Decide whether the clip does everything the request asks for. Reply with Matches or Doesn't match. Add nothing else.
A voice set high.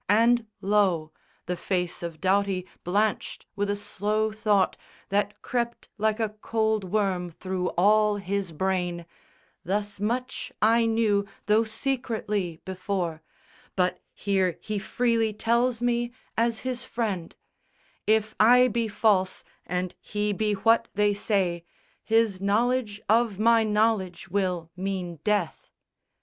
Matches